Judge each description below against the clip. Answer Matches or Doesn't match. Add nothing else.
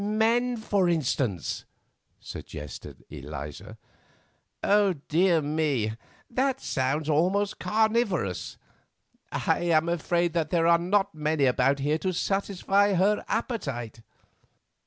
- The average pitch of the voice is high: Doesn't match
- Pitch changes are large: Matches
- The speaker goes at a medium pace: Doesn't match